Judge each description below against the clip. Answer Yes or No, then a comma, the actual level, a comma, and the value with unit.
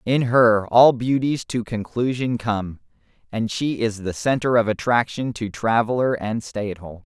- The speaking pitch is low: Yes, low, 115 Hz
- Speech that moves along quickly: No, average, 170 wpm